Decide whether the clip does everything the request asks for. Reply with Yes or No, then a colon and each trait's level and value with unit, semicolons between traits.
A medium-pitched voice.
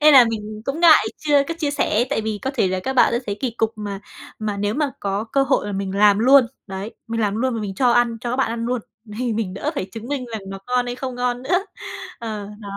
No: high, 230 Hz